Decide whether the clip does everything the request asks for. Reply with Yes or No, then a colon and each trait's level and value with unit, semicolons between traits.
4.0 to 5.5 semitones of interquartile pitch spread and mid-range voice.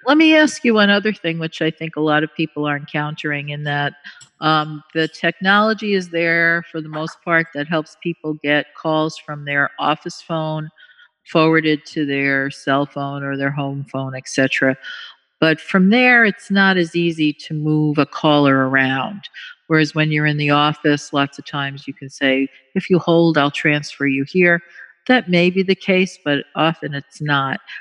No: average, 3.0 semitones; medium, 155 Hz